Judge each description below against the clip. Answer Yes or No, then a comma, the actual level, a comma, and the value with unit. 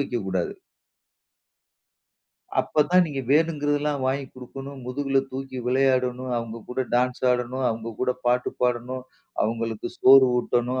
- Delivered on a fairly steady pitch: Yes, narrow, 1.9 semitones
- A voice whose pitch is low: Yes, low, 130 Hz